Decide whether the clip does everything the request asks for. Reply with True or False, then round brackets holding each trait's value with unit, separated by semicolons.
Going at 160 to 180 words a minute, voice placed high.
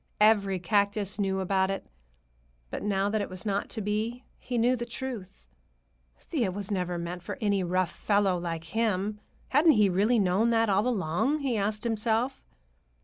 True (165 wpm; 205 Hz)